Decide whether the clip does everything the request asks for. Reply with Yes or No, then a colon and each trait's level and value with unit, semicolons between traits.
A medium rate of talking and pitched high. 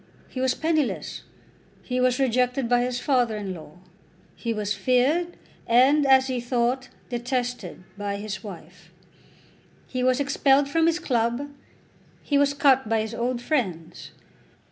Yes: average, 145 wpm; very high, 250 Hz